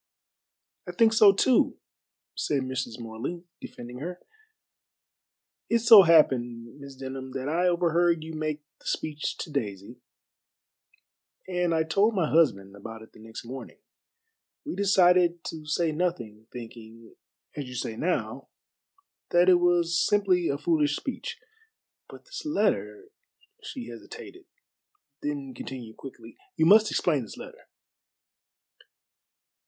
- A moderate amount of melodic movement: No, wide, 6.3 semitones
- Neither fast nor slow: No, slow, 125 wpm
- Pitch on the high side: No, medium, 155 Hz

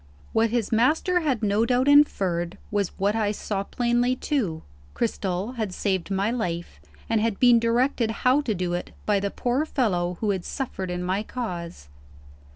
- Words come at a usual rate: Yes, average, 170 wpm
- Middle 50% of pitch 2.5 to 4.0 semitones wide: No, average, 4.6 semitones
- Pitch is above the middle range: Yes, high, 220 Hz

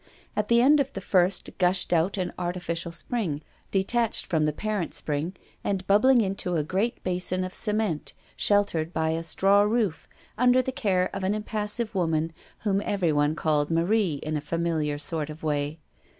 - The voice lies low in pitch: No, medium, 185 Hz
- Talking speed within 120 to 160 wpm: No, average, 170 wpm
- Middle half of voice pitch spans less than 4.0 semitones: No, average, 4.5 semitones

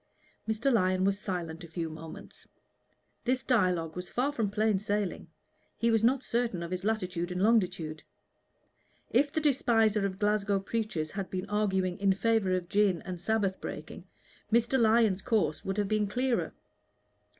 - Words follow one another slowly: No, average, 160 wpm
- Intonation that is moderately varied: Yes, average, 3.5 semitones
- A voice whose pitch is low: No, high, 200 Hz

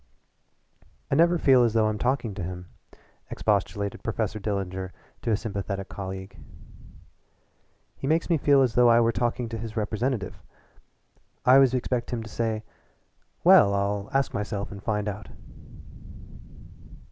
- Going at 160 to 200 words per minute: No, average, 145 wpm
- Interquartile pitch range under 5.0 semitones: Yes, average, 3.7 semitones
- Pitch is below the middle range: Yes, low, 110 Hz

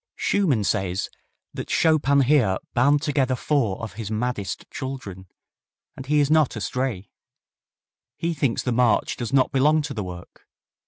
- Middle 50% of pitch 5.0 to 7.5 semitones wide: Yes, wide, 5.4 semitones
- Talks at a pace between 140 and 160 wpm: Yes, average, 150 wpm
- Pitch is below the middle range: Yes, low, 130 Hz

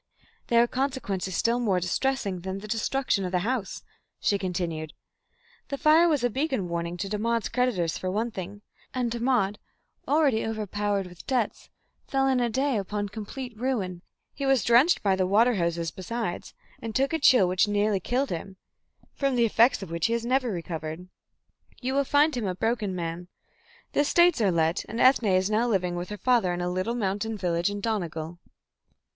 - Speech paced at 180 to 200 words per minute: Yes, average, 185 wpm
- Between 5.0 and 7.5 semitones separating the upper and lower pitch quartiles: Yes, average, 5.3 semitones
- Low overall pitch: No, high, 210 Hz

